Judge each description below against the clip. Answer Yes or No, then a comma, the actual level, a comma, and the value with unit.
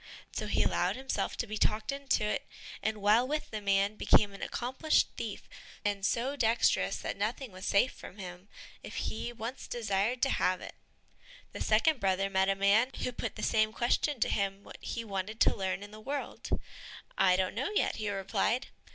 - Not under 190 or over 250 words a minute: Yes, average, 195 wpm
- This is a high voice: Yes, high, 215 Hz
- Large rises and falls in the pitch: No, average, 3.7 semitones